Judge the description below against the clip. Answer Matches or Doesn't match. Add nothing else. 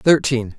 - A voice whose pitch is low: Matches